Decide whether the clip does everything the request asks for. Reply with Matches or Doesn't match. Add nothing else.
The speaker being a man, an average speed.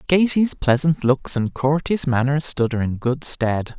Matches